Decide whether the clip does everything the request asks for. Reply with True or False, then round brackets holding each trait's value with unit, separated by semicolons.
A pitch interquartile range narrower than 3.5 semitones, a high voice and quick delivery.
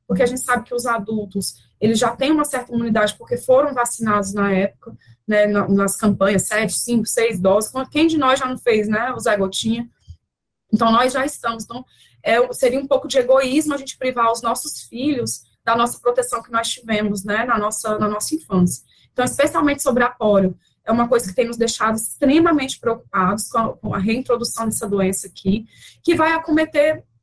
False (3.8 semitones; 230 Hz; 195 wpm)